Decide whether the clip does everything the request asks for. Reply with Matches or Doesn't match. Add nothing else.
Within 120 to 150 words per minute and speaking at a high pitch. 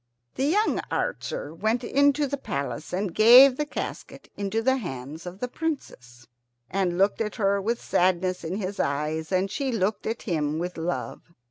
Doesn't match